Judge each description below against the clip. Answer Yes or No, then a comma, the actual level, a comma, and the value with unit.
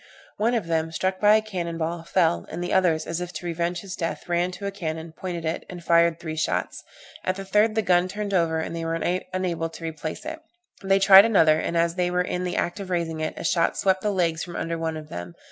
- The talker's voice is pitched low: No, medium, 175 Hz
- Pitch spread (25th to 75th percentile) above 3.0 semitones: No, narrow, 2.4 semitones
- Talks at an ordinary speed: No, fast, 250 wpm